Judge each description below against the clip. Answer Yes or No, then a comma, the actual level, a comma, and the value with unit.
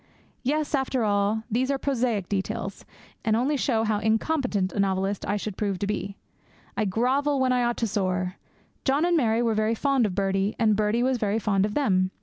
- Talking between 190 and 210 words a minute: Yes, average, 200 wpm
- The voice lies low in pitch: No, high, 220 Hz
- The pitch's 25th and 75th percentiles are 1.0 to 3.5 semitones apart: No, average, 4.2 semitones